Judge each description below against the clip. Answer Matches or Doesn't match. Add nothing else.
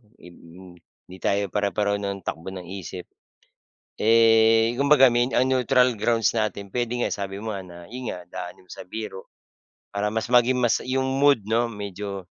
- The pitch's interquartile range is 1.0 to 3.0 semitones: Doesn't match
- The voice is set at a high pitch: Doesn't match